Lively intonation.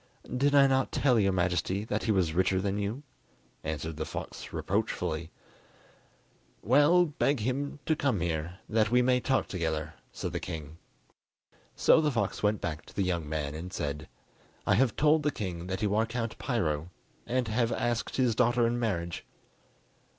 Yes: wide, 6.7 semitones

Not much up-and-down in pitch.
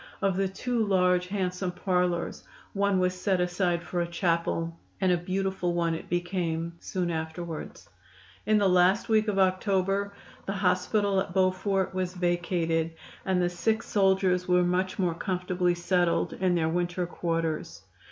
Yes: narrow, 1.7 semitones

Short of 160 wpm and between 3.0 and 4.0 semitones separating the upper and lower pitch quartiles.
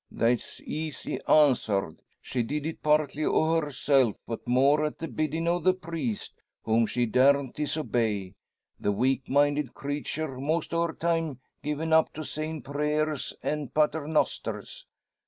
Yes: average, 140 wpm; average, 3.5 semitones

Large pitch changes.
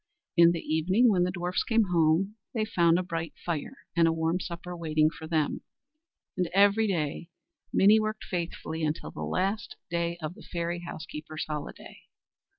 No: average, 2.9 semitones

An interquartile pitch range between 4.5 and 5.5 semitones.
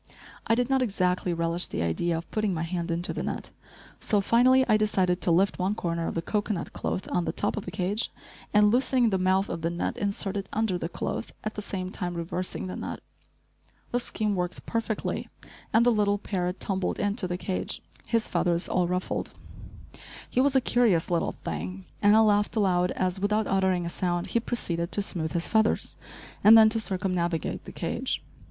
No: average, 3.4 semitones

